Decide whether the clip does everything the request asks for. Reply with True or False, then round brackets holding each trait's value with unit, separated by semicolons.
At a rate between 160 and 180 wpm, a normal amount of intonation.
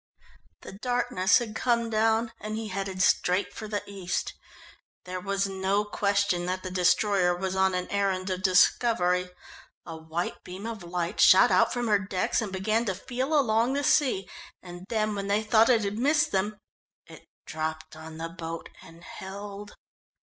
True (170 wpm; 3.2 semitones)